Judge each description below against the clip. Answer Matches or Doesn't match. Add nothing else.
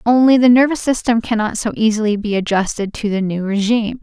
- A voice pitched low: Doesn't match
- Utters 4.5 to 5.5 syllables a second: Doesn't match